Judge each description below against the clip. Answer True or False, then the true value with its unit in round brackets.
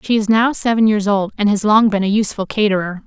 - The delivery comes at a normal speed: False (255 wpm)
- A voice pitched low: False (210 Hz)